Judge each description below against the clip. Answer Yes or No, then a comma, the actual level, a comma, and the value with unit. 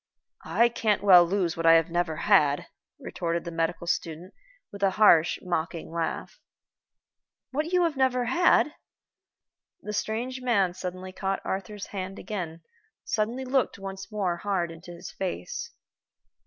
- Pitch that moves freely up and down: No, average, 4.1 semitones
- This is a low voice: No, high, 190 Hz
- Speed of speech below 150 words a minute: Yes, average, 140 wpm